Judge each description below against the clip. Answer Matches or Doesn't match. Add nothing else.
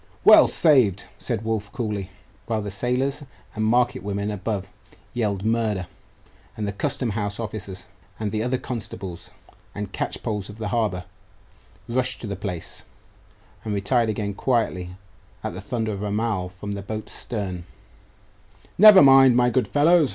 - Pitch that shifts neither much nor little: Matches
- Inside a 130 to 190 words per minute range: Matches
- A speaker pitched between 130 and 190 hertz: Doesn't match